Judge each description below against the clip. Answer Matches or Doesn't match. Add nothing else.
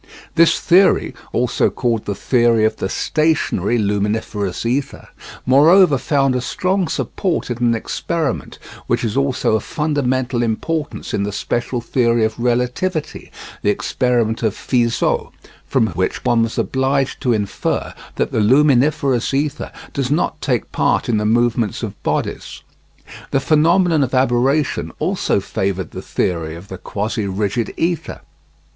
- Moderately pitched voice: Doesn't match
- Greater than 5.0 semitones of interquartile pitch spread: Doesn't match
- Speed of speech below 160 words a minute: Matches